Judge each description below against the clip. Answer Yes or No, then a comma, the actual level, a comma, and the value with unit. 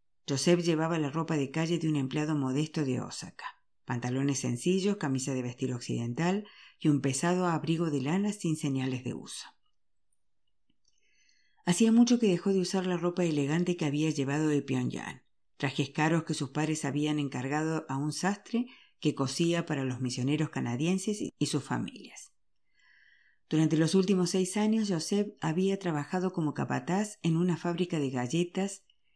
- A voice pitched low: No, medium, 160 Hz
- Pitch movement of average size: Yes, average, 4.6 semitones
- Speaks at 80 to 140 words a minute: No, average, 155 wpm